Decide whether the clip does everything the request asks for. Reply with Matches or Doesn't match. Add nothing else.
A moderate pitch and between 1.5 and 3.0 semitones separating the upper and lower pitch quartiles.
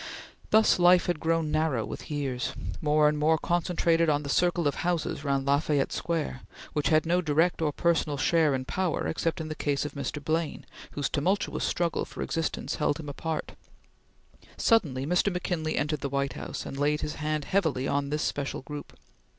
Matches